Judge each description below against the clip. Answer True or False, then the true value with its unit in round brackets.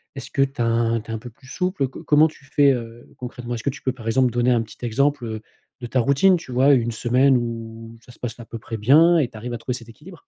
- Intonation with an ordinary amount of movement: True (3.1 semitones)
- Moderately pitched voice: False (120 Hz)